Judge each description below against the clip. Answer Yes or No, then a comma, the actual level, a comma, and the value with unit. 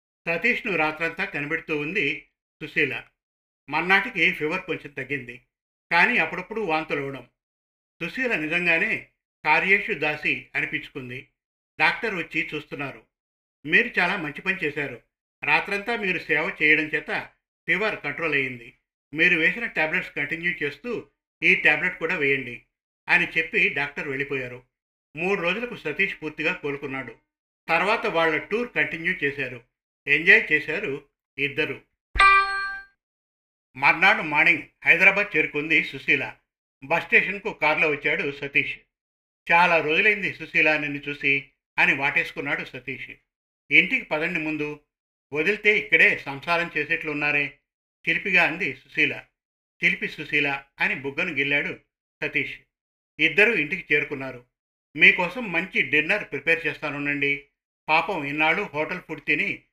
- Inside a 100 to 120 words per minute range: Yes, average, 105 wpm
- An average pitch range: Yes, average, 3.4 semitones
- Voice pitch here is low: No, medium, 155 Hz